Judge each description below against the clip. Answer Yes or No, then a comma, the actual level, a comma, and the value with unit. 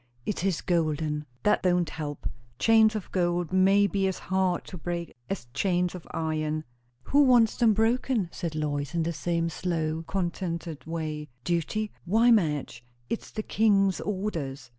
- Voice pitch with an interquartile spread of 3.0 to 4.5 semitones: Yes, average, 4.1 semitones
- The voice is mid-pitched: Yes, medium, 175 Hz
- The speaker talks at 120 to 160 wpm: Yes, average, 155 wpm